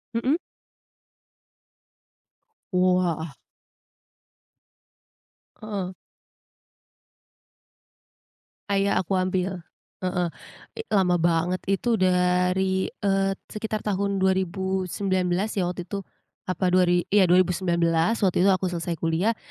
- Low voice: No, medium, 185 Hz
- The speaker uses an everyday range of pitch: No, narrow, 1.6 semitones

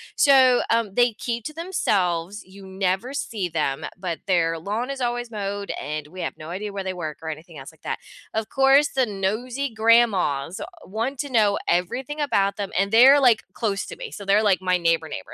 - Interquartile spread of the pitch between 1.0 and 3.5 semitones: No, average, 5.2 semitones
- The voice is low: No, high, 200 Hz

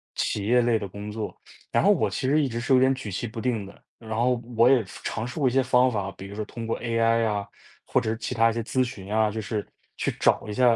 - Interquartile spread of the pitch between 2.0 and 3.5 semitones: Yes, average, 2.7 semitones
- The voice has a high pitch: No, low, 115 Hz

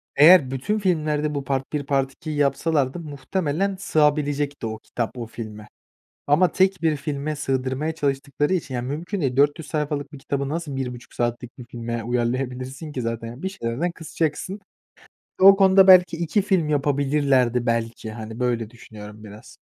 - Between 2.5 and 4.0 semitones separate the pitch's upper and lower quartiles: No, average, 4.4 semitones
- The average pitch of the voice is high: No, medium, 140 Hz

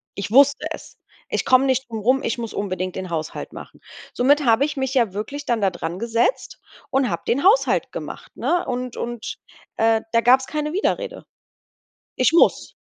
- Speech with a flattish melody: No, average, 3.9 semitones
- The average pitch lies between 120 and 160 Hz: No, high, 245 Hz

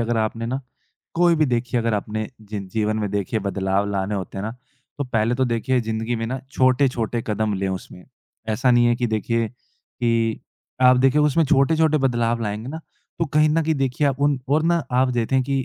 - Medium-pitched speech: No, low, 120 Hz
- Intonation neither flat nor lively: Yes, average, 3.6 semitones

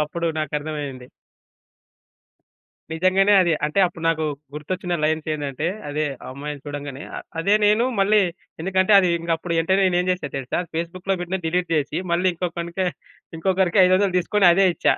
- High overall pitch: No, medium, 170 Hz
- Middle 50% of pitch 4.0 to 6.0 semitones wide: No, average, 3.6 semitones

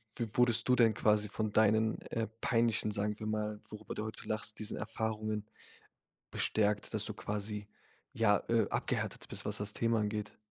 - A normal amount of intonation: No, narrow, 1.1 semitones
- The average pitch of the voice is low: Yes, low, 110 Hz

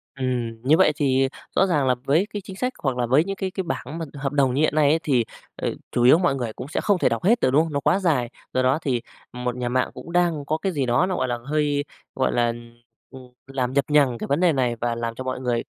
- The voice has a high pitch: No, low, 135 Hz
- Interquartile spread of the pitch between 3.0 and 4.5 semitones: Yes, average, 4.2 semitones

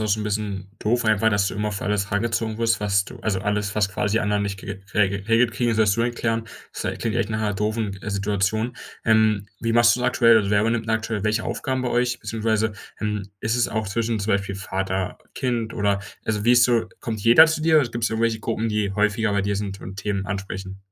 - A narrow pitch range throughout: Yes, narrow, 2.2 semitones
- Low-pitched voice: Yes, low, 110 Hz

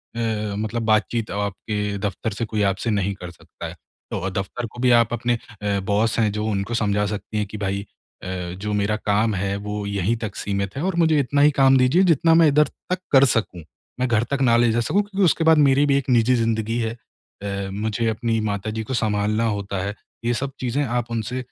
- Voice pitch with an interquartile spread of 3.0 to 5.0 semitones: Yes, average, 3.7 semitones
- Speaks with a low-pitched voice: Yes, low, 110 Hz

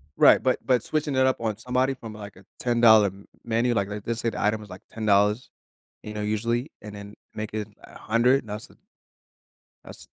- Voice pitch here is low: Yes, low, 110 Hz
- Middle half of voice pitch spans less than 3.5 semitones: Yes, narrow, 2.5 semitones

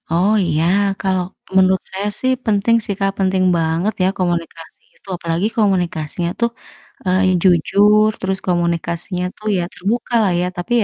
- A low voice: No, medium, 185 Hz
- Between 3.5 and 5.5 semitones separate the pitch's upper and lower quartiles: No, average, 2.8 semitones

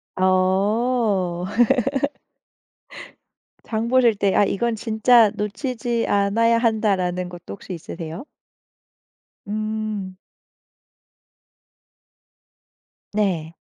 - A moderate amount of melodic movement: Yes, average, 3.6 semitones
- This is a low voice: No, high, 210 Hz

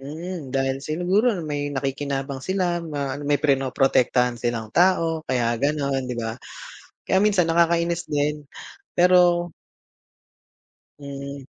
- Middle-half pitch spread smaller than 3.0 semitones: No, average, 4.3 semitones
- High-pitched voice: No, medium, 145 Hz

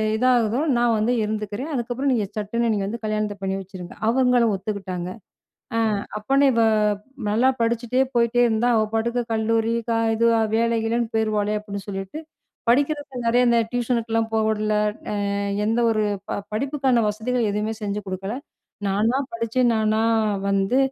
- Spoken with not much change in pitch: Yes, narrow, 2.3 semitones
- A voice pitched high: Yes, high, 225 Hz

